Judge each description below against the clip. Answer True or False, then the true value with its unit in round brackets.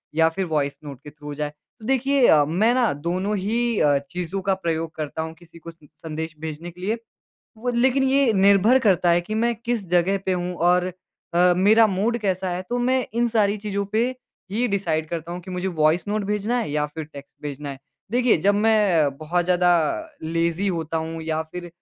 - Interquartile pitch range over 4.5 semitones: True (5.0 semitones)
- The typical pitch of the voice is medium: True (180 Hz)